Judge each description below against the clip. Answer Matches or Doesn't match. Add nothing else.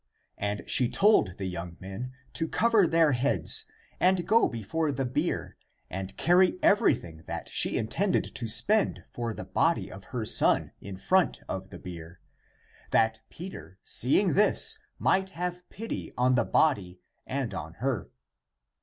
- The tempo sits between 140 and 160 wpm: Matches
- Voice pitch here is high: Doesn't match